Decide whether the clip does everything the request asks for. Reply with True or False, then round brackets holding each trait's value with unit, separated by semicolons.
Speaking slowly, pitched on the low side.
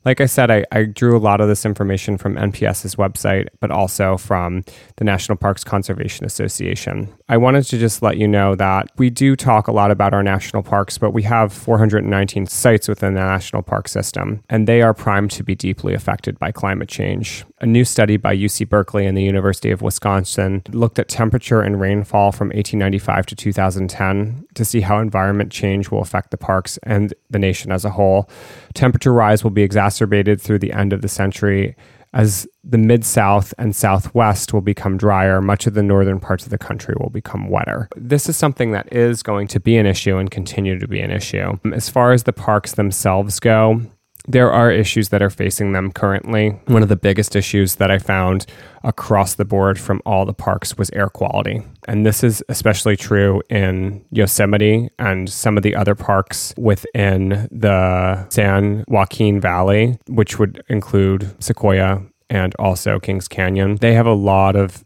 False (190 wpm; 105 Hz)